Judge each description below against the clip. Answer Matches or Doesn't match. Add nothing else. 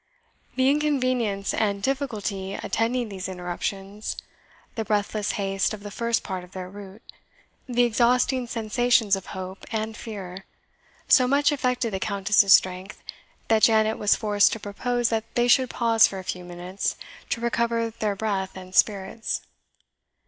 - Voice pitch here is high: Matches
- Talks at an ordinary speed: Matches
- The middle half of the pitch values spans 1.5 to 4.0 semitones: Matches